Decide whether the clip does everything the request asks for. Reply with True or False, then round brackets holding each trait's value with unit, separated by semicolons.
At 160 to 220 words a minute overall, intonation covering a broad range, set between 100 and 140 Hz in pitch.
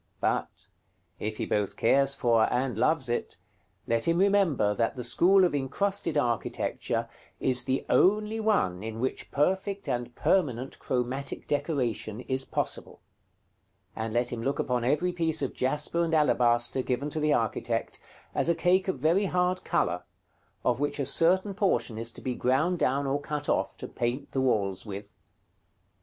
True (165 wpm; 6.0 semitones; 135 Hz)